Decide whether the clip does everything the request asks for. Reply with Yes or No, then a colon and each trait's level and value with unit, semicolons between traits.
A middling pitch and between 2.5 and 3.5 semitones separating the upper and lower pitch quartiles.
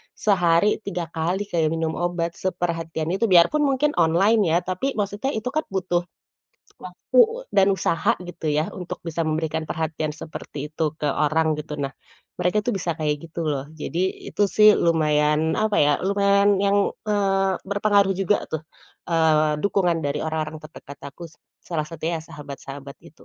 No: medium, 170 Hz; average, 4.1 semitones